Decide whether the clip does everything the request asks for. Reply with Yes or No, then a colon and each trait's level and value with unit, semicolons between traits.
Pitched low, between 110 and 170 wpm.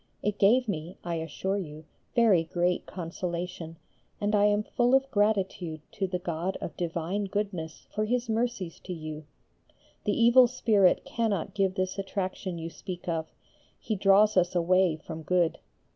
No: medium, 185 Hz; average, 160 wpm